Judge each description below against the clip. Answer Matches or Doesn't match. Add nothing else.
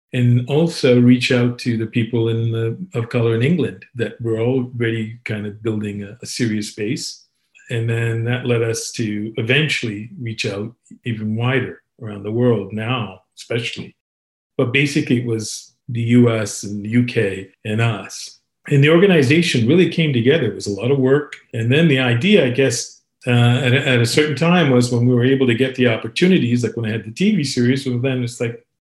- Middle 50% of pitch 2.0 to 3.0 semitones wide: Matches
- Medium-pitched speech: Doesn't match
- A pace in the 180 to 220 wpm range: Matches